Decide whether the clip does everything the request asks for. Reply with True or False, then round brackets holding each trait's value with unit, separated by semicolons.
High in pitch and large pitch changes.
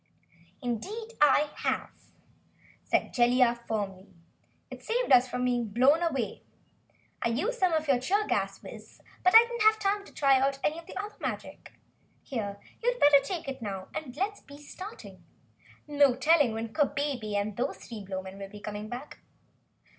True (270 Hz; 6.6 semitones)